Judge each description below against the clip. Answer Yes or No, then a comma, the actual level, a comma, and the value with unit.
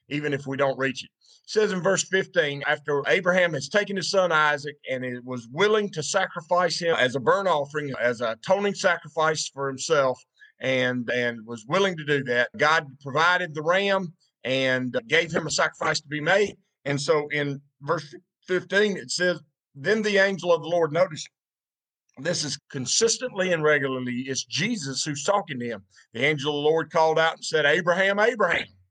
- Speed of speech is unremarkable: Yes, average, 185 wpm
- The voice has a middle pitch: Yes, medium, 155 Hz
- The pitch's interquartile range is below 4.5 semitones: No, average, 5.1 semitones